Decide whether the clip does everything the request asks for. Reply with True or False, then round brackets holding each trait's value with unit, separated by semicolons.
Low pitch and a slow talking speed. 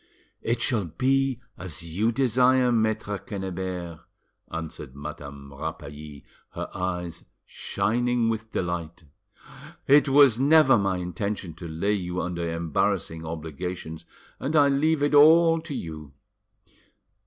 True (95 Hz; 120 wpm)